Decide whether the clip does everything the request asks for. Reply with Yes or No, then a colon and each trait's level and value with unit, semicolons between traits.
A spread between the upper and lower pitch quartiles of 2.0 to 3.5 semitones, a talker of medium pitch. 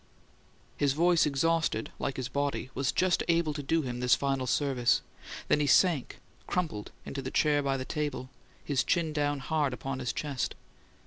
Yes: average, 2.9 semitones; medium, 145 Hz